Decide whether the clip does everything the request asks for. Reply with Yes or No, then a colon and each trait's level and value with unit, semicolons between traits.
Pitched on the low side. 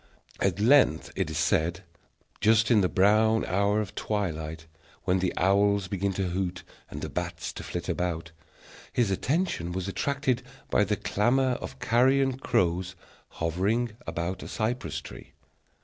Yes: low, 100 Hz